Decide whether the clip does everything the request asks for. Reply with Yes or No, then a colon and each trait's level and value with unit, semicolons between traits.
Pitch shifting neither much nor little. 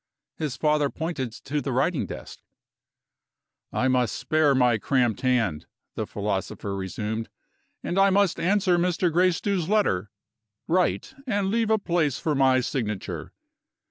No: wide, 6.5 semitones